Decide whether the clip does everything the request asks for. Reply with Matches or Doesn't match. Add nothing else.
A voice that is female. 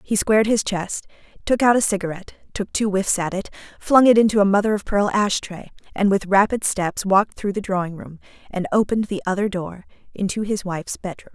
Matches